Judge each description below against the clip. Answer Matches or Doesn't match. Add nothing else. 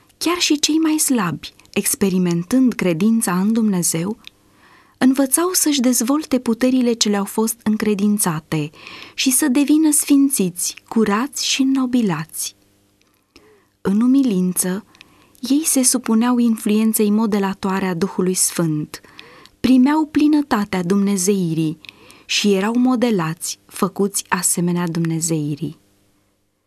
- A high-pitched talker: Matches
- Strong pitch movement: Matches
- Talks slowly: Matches